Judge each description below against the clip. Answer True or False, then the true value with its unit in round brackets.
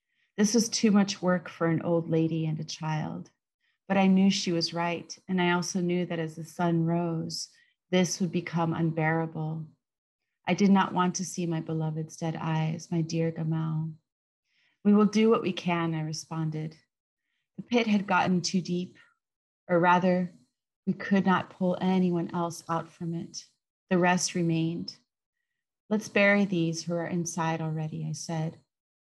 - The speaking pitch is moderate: True (170 Hz)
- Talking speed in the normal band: True (165 wpm)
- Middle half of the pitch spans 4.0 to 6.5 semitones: False (2.4 semitones)